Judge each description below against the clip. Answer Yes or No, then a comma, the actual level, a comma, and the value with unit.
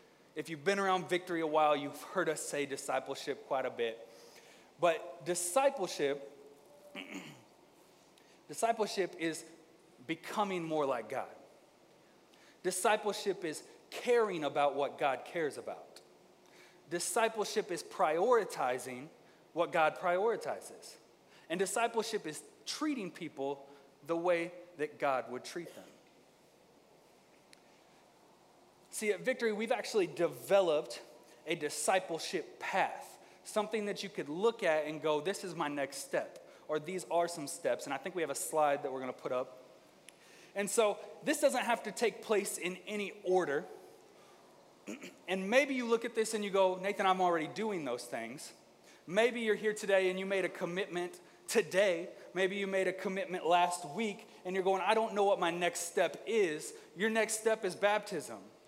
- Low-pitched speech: No, medium, 185 Hz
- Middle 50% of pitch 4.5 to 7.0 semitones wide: Yes, average, 5.0 semitones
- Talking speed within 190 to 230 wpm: No, average, 150 wpm